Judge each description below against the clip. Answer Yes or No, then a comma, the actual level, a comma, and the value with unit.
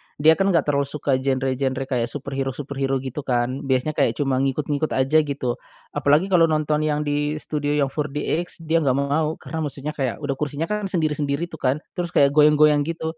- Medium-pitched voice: Yes, medium, 145 Hz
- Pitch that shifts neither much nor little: No, narrow, 2.2 semitones